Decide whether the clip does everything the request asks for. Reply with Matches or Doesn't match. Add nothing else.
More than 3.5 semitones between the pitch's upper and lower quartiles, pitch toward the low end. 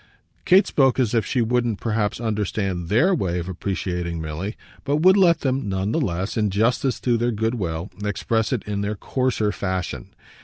Matches